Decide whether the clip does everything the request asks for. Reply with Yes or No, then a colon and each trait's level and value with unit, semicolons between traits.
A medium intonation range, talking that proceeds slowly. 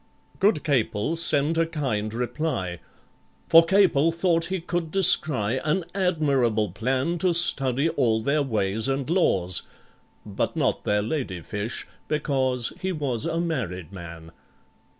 No: wide, 7.2 semitones; slow, 130 wpm